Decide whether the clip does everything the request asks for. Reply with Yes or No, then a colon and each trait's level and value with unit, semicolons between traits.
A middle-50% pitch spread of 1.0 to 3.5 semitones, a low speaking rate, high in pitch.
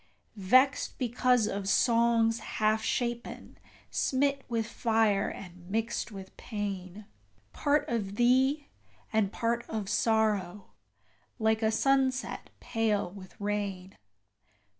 Yes: average, 3.0 semitones; slow, 105 wpm; high, 220 Hz